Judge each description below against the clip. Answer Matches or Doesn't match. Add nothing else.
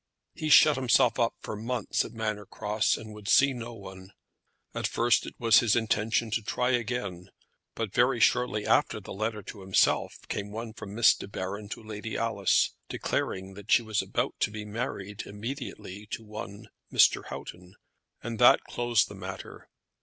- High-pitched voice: Doesn't match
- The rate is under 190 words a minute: Matches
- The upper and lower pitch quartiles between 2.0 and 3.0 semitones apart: Matches